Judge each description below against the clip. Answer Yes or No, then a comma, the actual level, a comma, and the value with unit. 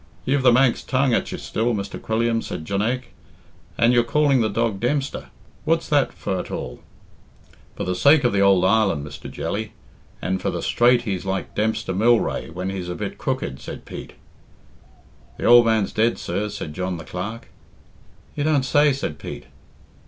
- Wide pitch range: No, average, 4.6 semitones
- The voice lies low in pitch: Yes, low, 110 Hz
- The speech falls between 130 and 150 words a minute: No, average, 175 wpm